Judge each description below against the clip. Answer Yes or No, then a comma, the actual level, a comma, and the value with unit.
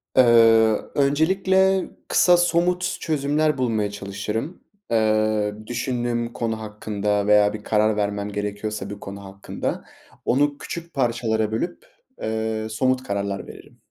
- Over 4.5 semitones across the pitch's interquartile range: Yes, average, 5.3 semitones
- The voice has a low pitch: Yes, low, 110 Hz